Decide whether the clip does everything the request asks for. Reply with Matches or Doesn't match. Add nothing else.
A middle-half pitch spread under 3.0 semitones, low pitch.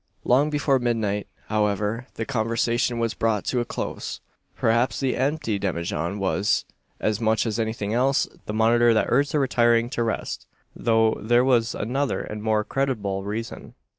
Matches